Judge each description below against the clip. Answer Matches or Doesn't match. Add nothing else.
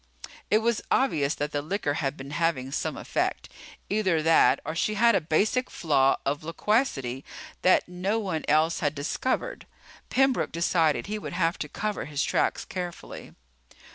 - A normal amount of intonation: Doesn't match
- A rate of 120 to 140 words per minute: Doesn't match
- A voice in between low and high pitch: Matches